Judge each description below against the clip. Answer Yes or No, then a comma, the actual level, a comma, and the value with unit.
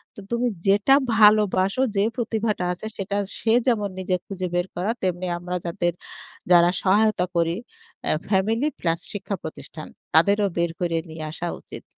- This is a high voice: Yes, high, 195 Hz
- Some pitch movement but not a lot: Yes, average, 3.4 semitones